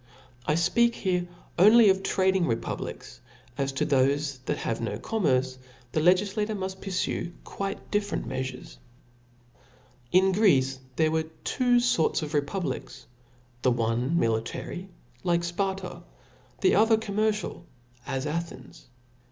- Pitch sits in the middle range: Yes, medium, 170 Hz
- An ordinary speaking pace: No, slow, 130 wpm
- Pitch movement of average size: No, wide, 6.7 semitones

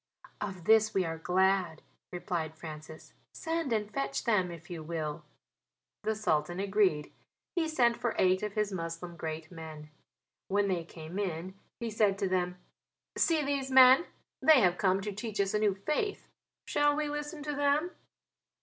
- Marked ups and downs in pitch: Yes, wide, 5.8 semitones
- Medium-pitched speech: No, high, 195 Hz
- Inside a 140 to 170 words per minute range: Yes, average, 165 wpm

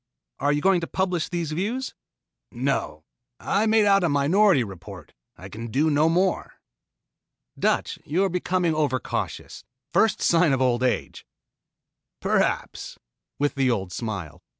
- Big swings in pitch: Yes, wide, 6.7 semitones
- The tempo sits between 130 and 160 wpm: Yes, average, 145 wpm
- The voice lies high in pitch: No, medium, 150 Hz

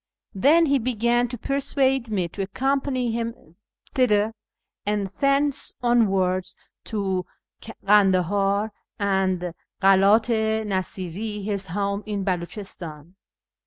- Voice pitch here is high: Yes, high, 210 Hz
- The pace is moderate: No, slow, 100 wpm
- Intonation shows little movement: No, average, 3.8 semitones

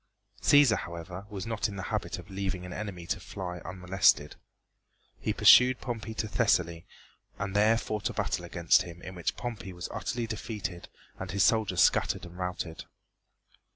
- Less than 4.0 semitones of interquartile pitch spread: Yes, average, 3.4 semitones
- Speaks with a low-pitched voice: Yes, very low, 95 Hz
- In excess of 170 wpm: No, average, 165 wpm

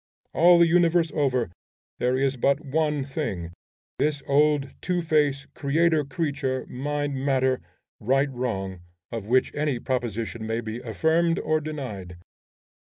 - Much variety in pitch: No, average, 3.6 semitones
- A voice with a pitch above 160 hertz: No, medium, 140 Hz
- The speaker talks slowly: Yes, slow, 130 wpm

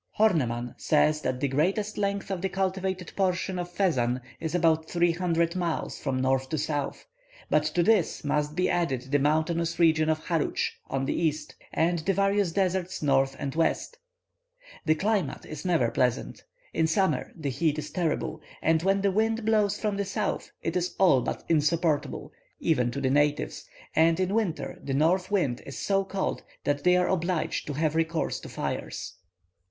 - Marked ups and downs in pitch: No, average, 4.1 semitones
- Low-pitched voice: No, medium, 165 Hz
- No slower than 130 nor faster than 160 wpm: No, average, 180 wpm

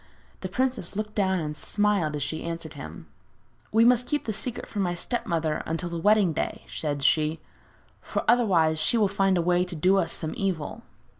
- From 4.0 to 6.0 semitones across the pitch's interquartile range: Yes, average, 4.8 semitones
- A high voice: No, medium, 180 Hz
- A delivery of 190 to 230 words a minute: Yes, average, 200 wpm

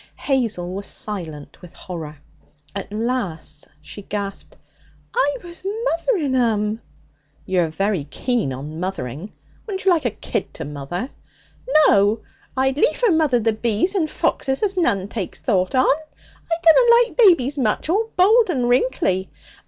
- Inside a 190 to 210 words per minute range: No, average, 145 wpm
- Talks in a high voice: Yes, high, 235 Hz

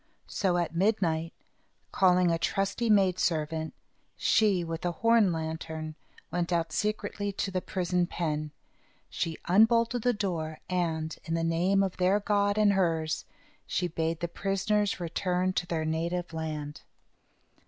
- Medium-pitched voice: Yes, medium, 175 Hz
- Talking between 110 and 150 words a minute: Yes, average, 145 wpm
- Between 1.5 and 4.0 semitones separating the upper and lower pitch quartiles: Yes, average, 3.3 semitones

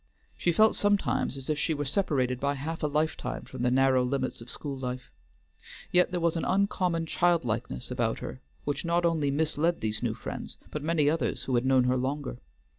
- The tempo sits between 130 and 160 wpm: No, average, 195 wpm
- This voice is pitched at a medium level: Yes, medium, 145 Hz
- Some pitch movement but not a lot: Yes, average, 4.4 semitones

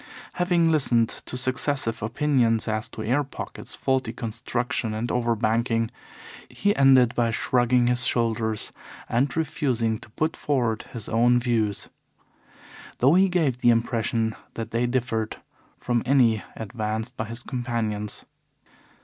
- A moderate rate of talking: No, slow, 130 wpm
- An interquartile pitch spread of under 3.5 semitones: Yes, narrow, 2.4 semitones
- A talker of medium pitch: No, low, 120 Hz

